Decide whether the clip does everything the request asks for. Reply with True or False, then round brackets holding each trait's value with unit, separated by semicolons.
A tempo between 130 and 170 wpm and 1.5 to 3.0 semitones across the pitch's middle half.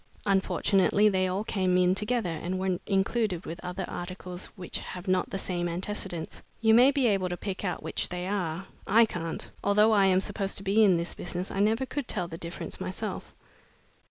False (195 wpm; 2.5 semitones)